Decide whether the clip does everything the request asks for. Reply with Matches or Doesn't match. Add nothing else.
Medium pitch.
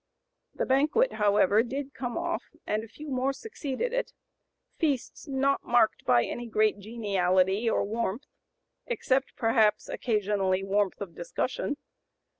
Doesn't match